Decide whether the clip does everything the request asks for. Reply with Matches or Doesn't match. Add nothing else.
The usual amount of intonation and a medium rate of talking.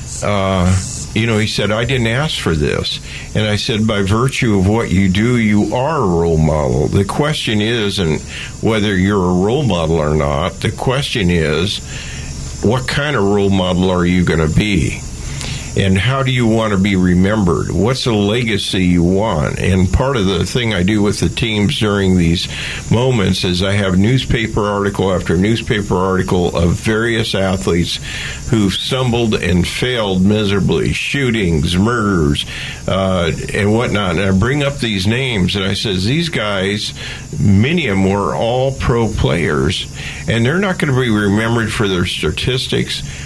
Matches